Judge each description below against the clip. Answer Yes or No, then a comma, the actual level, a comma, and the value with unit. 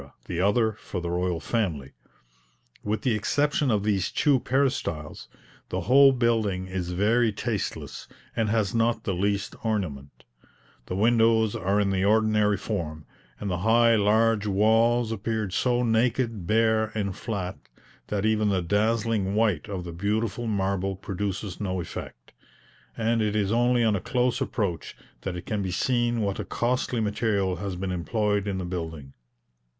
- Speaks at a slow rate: No, average, 155 wpm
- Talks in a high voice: No, low, 105 Hz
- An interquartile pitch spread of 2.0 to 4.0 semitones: Yes, average, 3.3 semitones